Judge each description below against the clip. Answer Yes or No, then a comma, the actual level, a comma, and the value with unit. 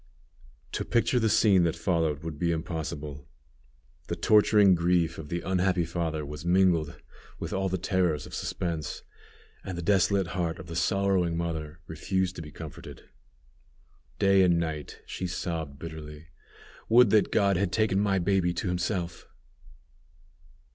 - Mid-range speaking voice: No, very low, 85 Hz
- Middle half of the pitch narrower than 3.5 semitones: Yes, average, 3.0 semitones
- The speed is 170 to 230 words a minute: No, average, 145 wpm